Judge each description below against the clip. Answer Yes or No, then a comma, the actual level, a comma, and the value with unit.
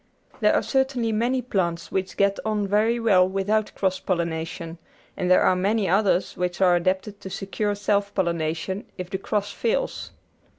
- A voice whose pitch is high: Yes, high, 195 Hz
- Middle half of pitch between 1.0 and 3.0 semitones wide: Yes, average, 2.7 semitones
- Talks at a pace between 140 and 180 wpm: Yes, average, 165 wpm